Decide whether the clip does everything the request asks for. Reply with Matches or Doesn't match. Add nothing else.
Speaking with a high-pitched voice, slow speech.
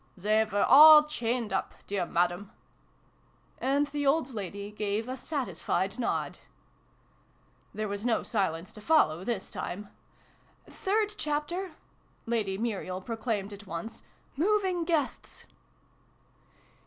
Matches